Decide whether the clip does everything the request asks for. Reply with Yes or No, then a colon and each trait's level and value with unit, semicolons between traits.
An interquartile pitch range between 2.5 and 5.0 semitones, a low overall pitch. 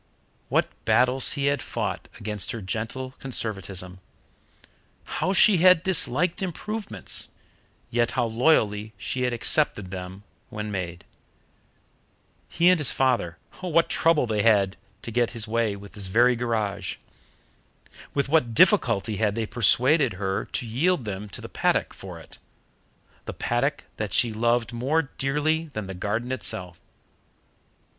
No: wide, 5.4 semitones; low, 120 Hz